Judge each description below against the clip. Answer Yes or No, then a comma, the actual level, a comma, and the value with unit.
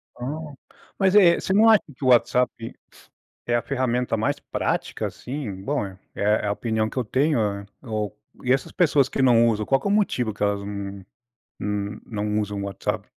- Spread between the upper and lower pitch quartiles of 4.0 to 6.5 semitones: Yes, average, 4.8 semitones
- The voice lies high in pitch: No, low, 115 Hz